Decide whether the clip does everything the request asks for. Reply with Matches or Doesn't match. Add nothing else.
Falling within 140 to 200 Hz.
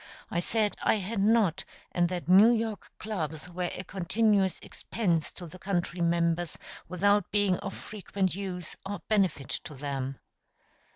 Matches